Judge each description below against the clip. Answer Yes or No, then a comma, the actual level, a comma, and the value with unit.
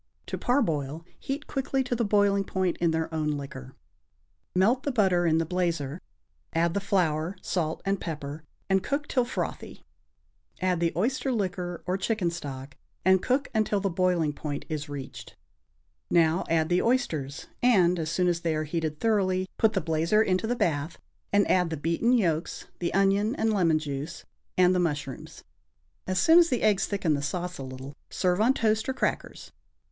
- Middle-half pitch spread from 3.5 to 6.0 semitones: Yes, average, 4.6 semitones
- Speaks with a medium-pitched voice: Yes, medium, 180 Hz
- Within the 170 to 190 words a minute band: Yes, average, 180 wpm